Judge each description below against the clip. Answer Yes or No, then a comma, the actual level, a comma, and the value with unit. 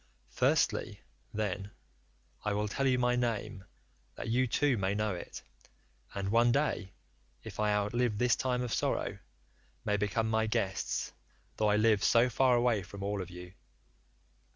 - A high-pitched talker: No, low, 110 Hz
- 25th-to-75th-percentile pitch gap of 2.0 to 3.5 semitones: Yes, average, 3.0 semitones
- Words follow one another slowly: No, average, 155 wpm